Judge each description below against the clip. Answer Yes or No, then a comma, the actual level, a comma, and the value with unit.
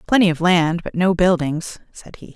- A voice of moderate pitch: Yes, medium, 175 Hz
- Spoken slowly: No, fast, 205 wpm